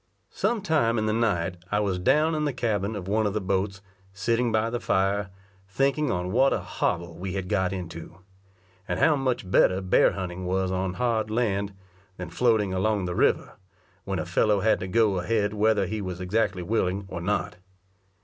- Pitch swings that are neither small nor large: Yes, average, 3.4 semitones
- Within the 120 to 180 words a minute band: No, average, 195 wpm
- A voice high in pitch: No, low, 100 Hz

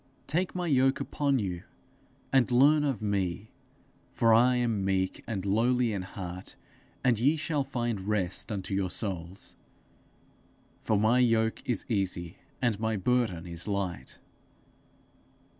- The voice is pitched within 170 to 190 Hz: No, low, 110 Hz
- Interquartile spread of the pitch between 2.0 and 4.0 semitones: No, average, 4.6 semitones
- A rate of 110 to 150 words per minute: Yes, slow, 135 wpm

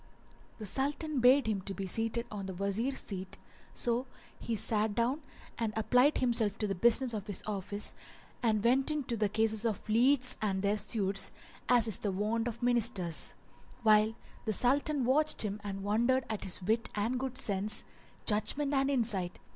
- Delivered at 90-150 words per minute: No, average, 170 wpm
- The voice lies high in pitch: Yes, high, 220 Hz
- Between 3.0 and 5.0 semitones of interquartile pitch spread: Yes, average, 3.4 semitones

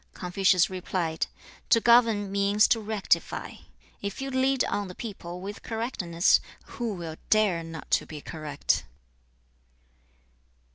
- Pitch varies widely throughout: No, average, 4.4 semitones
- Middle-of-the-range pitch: No, high, 200 Hz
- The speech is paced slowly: Yes, slow, 125 wpm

